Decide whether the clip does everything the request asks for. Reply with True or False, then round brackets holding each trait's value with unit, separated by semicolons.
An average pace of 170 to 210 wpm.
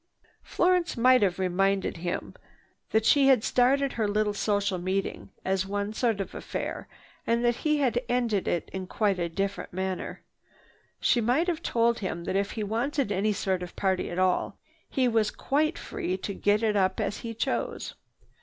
True (180 wpm)